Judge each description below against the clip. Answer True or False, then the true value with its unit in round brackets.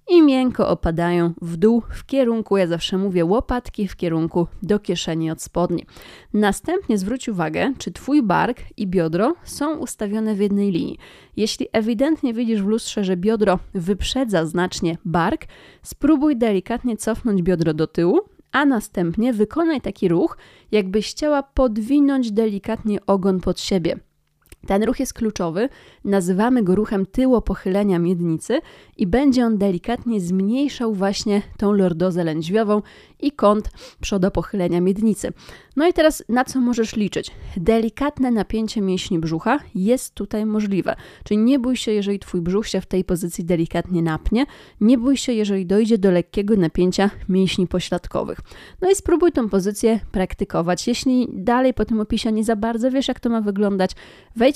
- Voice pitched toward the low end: False (210 Hz)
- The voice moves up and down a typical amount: True (4.7 semitones)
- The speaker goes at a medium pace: True (150 wpm)